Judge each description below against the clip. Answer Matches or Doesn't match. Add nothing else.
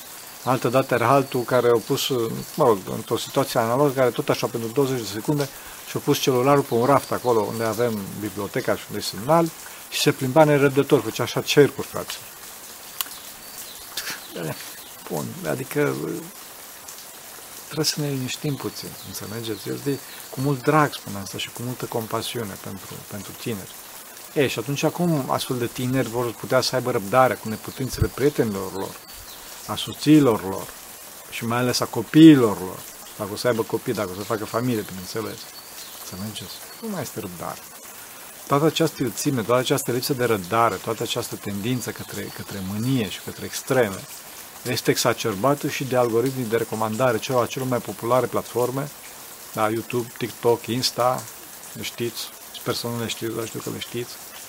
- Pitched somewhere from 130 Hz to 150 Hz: Doesn't match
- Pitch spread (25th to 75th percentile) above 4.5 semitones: Doesn't match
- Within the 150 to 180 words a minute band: Matches